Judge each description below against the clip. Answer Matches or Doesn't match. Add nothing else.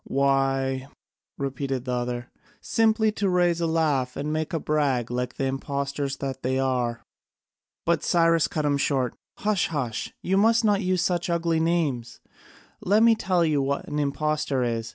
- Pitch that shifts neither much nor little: Matches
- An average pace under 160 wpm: Doesn't match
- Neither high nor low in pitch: Matches